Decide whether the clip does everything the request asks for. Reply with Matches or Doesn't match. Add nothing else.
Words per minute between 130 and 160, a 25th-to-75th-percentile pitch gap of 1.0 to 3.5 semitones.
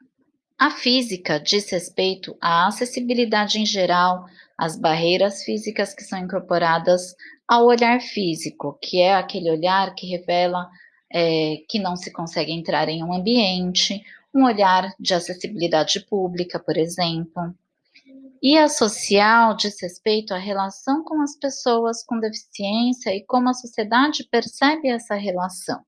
Doesn't match